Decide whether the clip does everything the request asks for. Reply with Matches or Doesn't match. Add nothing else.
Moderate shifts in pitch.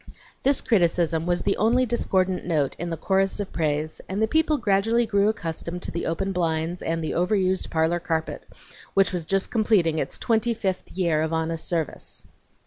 Matches